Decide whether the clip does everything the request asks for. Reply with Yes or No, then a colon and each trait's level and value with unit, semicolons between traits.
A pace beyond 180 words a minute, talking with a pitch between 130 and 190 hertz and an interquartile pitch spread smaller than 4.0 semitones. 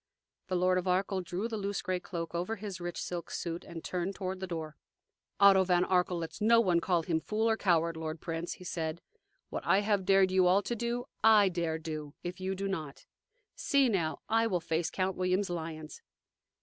Yes: fast, 205 wpm; medium, 185 Hz; average, 2.7 semitones